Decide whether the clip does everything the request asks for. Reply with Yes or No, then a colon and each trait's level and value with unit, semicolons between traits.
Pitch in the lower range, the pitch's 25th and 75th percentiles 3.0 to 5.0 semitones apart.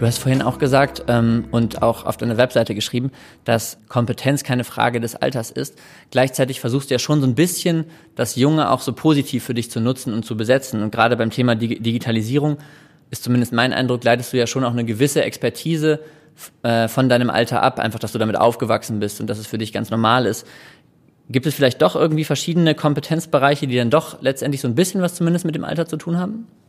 Yes: low, 130 Hz; average, 4.3 semitones